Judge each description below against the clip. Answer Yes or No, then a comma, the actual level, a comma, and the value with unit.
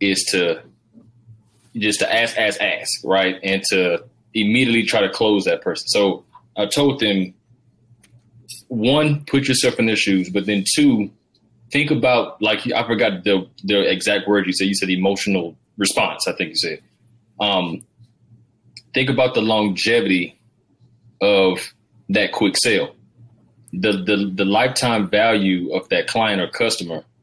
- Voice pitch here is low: Yes, low, 115 Hz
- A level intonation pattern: No, average, 3.4 semitones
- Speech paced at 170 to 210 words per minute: No, average, 150 wpm